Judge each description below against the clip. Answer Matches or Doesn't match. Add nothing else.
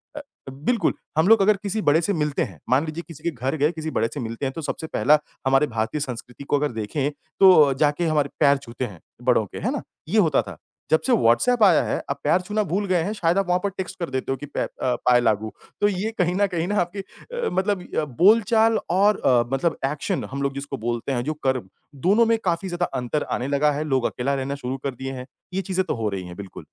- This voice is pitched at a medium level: Matches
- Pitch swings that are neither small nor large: Doesn't match